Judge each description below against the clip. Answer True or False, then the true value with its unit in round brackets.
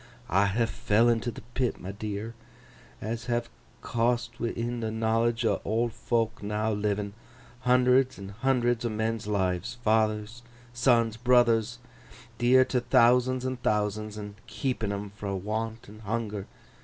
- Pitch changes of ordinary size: False (2.2 semitones)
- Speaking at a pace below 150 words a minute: True (140 wpm)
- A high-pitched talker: False (115 Hz)